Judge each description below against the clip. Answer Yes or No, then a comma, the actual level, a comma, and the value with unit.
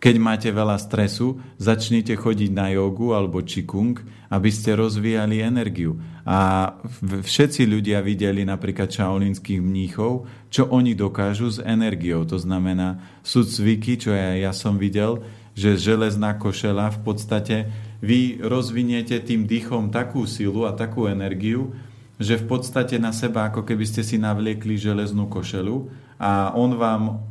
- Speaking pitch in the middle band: No, low, 110 Hz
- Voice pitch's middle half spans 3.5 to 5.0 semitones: No, narrow, 2.6 semitones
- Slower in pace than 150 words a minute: Yes, average, 140 wpm